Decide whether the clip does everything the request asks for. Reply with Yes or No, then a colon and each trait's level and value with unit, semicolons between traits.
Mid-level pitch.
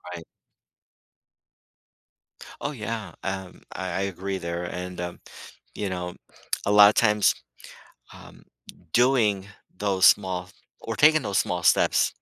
No: very low, 95 Hz